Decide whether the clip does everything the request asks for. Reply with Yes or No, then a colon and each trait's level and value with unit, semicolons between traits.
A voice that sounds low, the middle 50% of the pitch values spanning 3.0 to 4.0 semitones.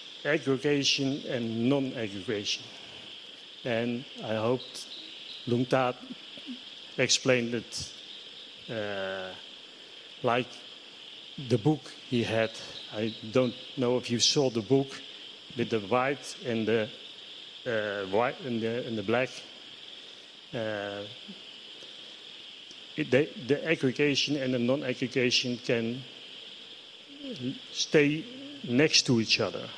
Yes: low, 125 Hz; average, 3.4 semitones